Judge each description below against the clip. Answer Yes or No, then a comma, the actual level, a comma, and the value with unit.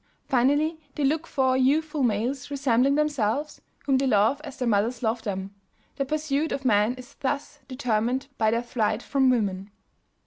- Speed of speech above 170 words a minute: No, average, 165 wpm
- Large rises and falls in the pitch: No, average, 4.0 semitones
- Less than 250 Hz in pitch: No, very high, 260 Hz